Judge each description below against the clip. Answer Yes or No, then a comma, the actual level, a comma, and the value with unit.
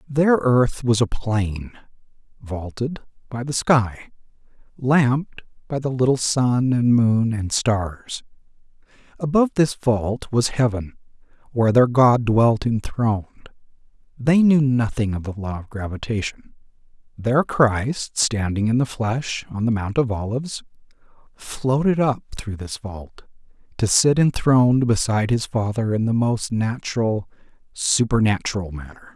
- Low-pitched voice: Yes, low, 115 Hz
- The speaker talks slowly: Yes, slow, 130 wpm